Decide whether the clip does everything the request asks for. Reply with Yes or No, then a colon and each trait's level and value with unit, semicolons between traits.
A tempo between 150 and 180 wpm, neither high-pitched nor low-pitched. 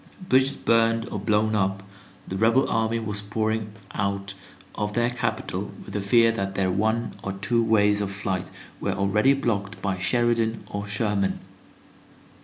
No: average, 155 wpm; low, 105 Hz